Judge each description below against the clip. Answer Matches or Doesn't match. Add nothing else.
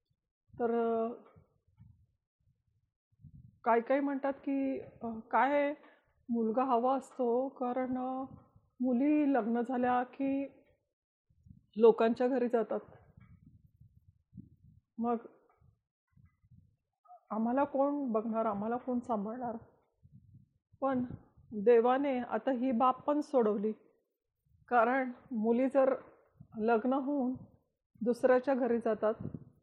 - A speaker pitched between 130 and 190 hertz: Doesn't match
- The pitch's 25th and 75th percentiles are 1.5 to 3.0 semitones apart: Matches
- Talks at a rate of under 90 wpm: Matches